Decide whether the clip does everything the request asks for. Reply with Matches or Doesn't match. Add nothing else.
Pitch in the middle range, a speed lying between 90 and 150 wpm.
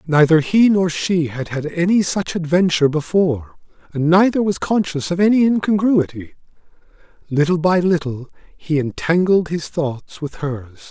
Matches